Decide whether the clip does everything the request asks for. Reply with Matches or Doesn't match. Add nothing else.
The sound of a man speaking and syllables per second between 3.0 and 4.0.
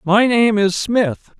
Matches